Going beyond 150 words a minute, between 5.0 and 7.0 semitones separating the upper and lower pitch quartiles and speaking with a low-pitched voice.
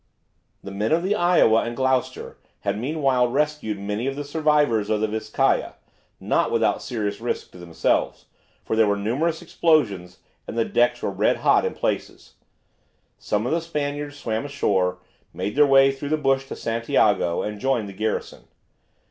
Yes: average, 170 wpm; wide, 5.5 semitones; low, 120 Hz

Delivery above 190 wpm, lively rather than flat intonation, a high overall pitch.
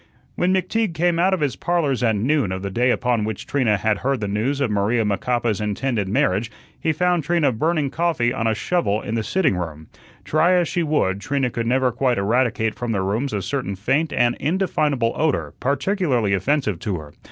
No: average, 200 wpm; wide, 6.5 semitones; low, 125 Hz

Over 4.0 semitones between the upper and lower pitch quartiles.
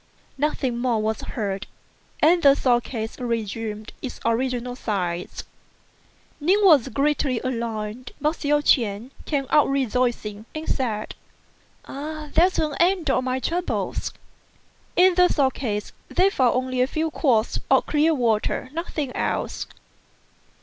Yes: average, 4.9 semitones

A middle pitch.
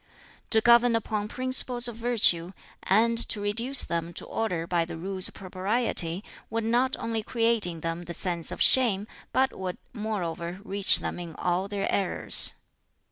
No: high, 205 Hz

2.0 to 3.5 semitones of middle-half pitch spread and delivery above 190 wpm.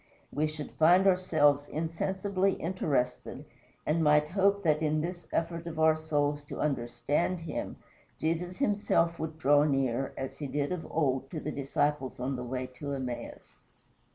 No: average, 3.0 semitones; average, 155 wpm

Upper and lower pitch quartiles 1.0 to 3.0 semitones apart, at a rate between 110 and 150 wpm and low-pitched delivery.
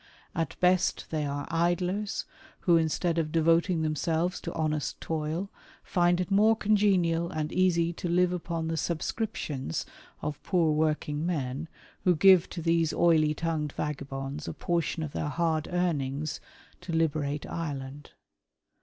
No: narrow, 2.5 semitones; average, 145 wpm; medium, 165 Hz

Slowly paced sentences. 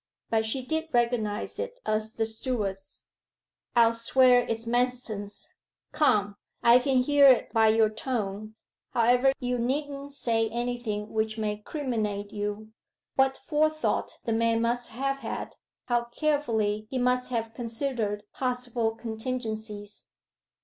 Yes: slow, 130 wpm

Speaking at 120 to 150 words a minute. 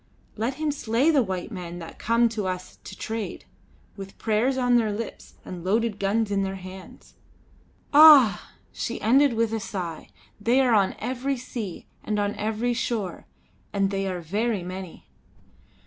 No: average, 165 wpm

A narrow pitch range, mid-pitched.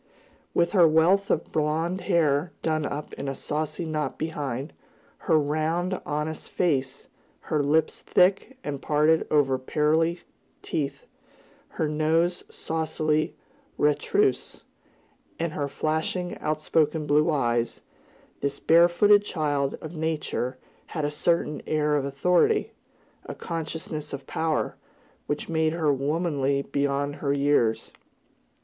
Yes: narrow, 2.2 semitones; medium, 155 Hz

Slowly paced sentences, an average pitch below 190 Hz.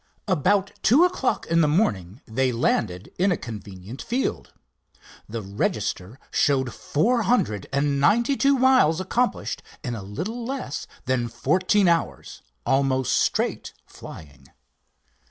Yes: slow, 125 wpm; medium, 140 Hz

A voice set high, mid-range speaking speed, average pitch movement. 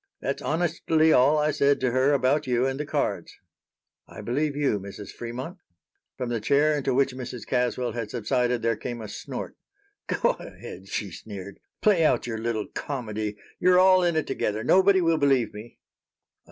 No: low, 130 Hz; average, 175 wpm; average, 4.7 semitones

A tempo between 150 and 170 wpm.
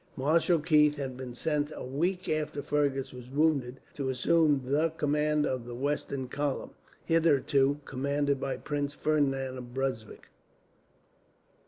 No: slow, 135 wpm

